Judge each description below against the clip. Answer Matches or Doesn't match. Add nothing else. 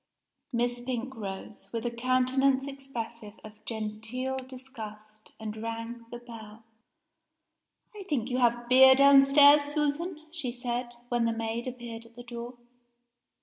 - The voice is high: Matches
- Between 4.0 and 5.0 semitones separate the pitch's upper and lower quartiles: Doesn't match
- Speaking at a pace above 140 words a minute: Doesn't match